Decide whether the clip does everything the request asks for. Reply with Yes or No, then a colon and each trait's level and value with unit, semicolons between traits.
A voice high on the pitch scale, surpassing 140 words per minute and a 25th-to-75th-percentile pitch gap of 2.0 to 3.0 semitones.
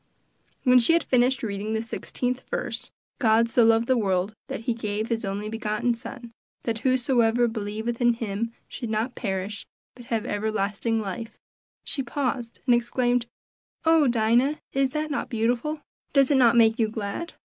Yes: high, 230 Hz; average, 165 wpm; narrow, 2.5 semitones